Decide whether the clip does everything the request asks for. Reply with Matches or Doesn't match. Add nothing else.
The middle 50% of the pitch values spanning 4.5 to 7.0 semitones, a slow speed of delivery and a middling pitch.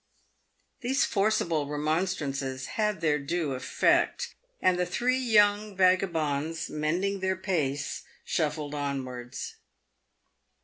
Matches